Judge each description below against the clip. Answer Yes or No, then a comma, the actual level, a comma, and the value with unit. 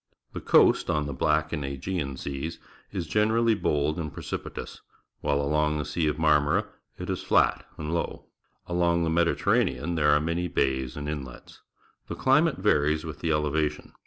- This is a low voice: Yes, very low, 75 Hz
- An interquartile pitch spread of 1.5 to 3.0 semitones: Yes, narrow, 2.4 semitones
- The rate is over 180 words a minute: No, average, 170 wpm